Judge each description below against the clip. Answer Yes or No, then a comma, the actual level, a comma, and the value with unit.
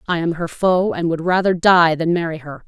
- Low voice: No, medium, 170 Hz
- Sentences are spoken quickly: Yes, fast, 245 wpm